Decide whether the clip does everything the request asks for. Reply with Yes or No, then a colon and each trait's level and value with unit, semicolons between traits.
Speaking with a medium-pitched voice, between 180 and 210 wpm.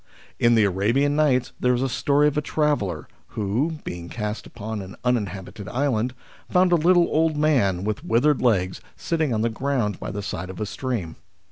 No: low, 120 Hz; average, 190 wpm